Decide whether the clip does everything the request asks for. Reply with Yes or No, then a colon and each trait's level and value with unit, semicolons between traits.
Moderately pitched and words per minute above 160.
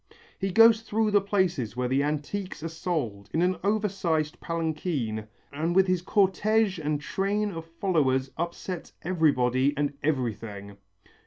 No: medium, 165 Hz; average, 145 wpm